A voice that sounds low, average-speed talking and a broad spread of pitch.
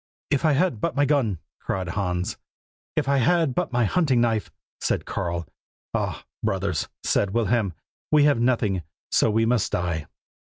Yes: low, 115 Hz; average, 160 wpm; wide, 6.4 semitones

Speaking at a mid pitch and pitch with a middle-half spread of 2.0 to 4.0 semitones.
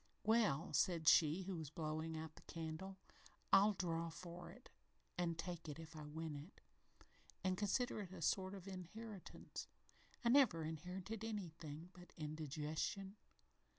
Yes: medium, 170 Hz; average, 3.4 semitones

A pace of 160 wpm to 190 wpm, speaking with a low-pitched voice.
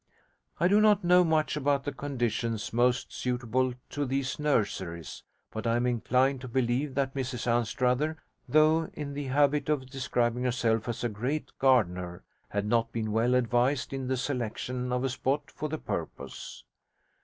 Yes: average, 165 wpm; low, 125 Hz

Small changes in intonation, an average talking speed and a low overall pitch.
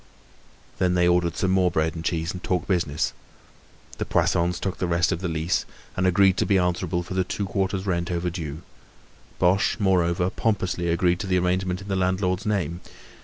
Yes: narrow, 1.5 semitones; average, 185 wpm; very low, 90 Hz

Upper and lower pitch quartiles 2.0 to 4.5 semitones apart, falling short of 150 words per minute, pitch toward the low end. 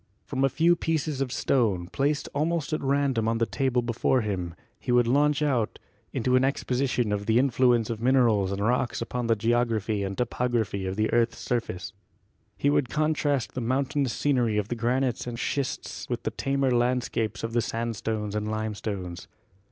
No: average, 3.6 semitones; average, 185 wpm; low, 120 Hz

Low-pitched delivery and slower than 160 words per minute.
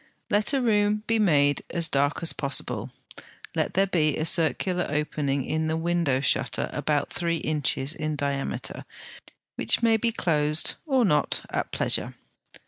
No: medium, 155 Hz; average, 150 wpm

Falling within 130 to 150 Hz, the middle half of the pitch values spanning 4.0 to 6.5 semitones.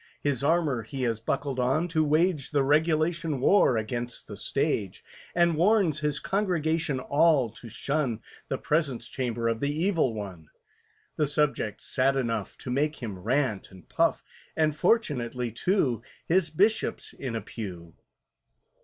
Yes: medium, 140 Hz; average, 5.1 semitones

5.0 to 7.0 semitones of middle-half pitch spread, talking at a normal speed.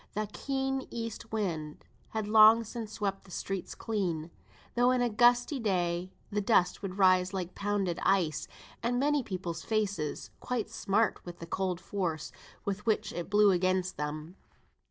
No: average, 3.7 semitones; average, 155 wpm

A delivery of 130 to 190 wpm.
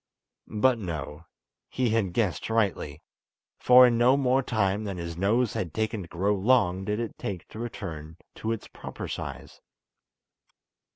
Yes: average, 155 wpm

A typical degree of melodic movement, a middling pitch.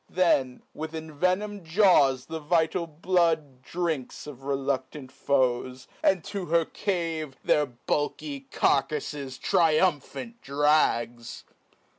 Yes: average, 4.0 semitones; medium, 150 Hz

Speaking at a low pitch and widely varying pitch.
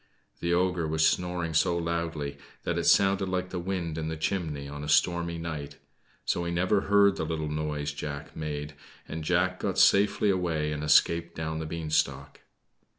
No: very low, 80 Hz; average, 2.8 semitones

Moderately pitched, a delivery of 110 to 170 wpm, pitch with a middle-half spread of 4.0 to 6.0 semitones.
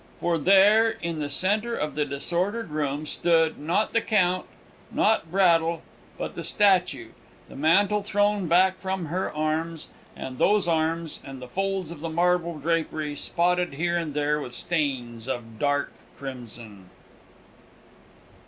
Yes: medium, 165 Hz; average, 145 wpm; average, 4.3 semitones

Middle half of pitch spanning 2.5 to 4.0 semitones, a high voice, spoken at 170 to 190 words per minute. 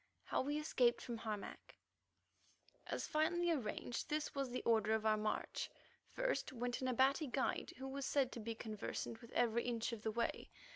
Yes: average, 3.6 semitones; high, 245 Hz; average, 180 wpm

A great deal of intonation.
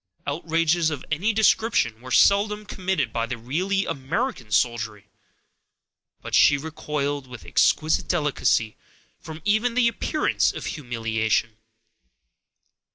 Yes: wide, 8.2 semitones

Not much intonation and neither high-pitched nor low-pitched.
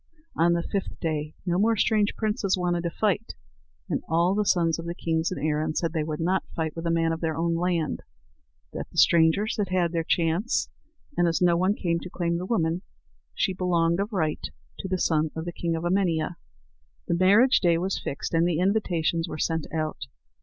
Yes: narrow, 2.3 semitones; medium, 170 Hz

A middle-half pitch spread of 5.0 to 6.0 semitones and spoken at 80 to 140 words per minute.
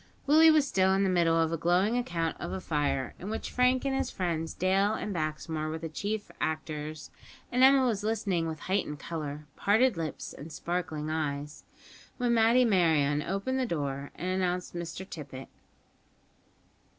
No: average, 5.3 semitones; average, 170 wpm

